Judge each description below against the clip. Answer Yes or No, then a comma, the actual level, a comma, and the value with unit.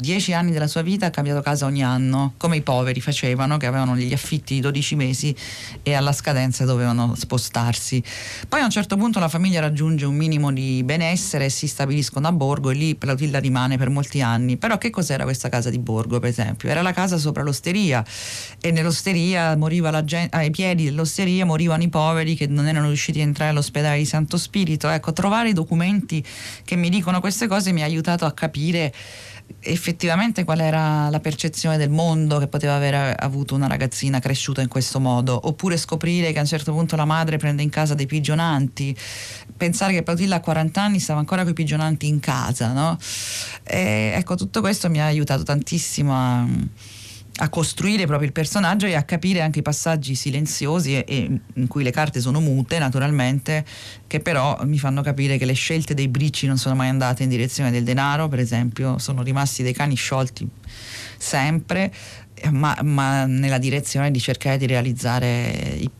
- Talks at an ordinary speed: No, fast, 190 wpm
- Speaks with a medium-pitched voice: Yes, medium, 145 Hz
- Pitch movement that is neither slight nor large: Yes, average, 3.9 semitones